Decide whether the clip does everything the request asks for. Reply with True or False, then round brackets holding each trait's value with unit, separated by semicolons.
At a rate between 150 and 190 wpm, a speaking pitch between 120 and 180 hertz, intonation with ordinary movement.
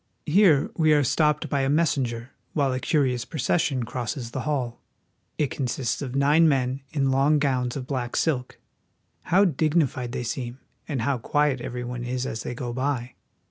True (175 wpm; 135 Hz; 3.1 semitones)